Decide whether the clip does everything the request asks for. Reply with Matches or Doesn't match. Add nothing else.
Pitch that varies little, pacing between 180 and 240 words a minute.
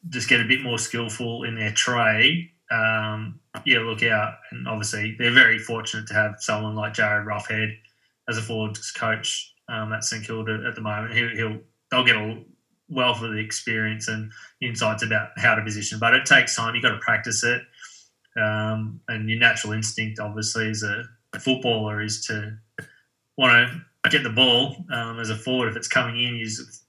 Matches